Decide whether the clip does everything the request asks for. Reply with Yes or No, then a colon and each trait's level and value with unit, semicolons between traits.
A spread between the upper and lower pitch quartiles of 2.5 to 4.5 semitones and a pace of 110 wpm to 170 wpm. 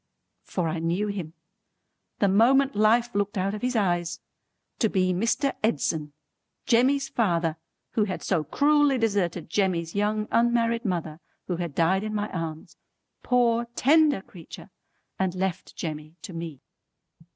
No: wide, 5.4 semitones; average, 140 wpm